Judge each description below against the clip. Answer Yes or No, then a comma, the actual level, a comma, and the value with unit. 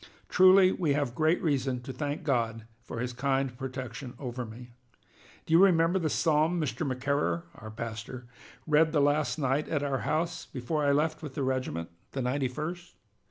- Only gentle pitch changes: No, average, 4.0 semitones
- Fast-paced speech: No, average, 175 wpm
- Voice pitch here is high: No, medium, 140 Hz